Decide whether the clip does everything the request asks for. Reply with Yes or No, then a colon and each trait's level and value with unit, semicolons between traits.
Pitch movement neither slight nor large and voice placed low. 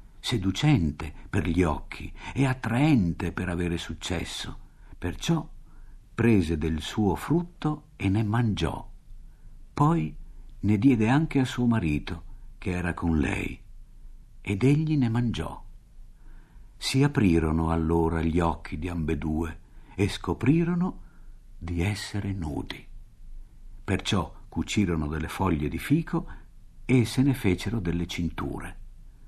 No: wide, 6.4 semitones; very low, 95 Hz